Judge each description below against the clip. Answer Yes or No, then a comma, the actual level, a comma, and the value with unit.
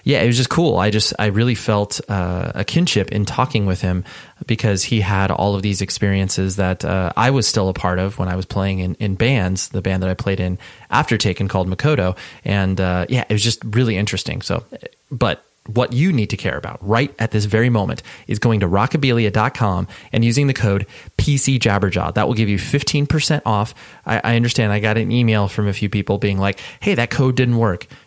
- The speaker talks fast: Yes, fast, 220 wpm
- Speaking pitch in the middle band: No, low, 105 Hz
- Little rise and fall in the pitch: No, average, 3.6 semitones